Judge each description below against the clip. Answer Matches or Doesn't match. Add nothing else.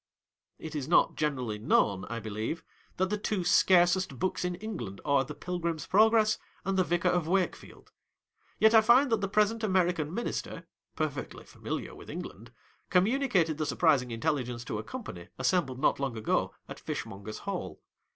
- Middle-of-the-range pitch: Matches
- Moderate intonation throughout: Doesn't match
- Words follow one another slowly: Doesn't match